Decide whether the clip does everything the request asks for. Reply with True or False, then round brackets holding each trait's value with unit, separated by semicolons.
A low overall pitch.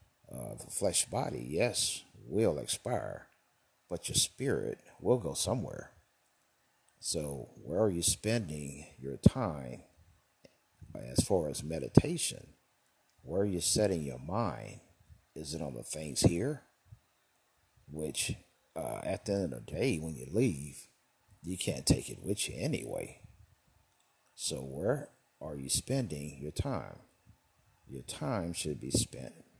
True (80 Hz)